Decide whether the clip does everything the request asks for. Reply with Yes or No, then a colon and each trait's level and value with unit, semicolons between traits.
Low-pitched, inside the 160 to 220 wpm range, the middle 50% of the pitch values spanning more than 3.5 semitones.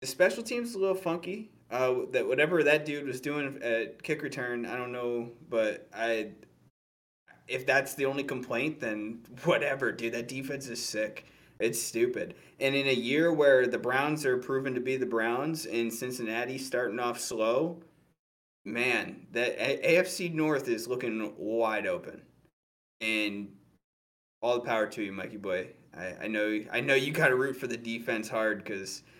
Yes: low, 125 Hz; average, 170 wpm; average, 4.3 semitones